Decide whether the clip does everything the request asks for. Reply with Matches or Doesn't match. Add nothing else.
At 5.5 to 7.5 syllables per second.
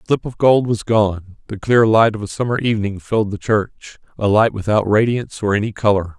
Matches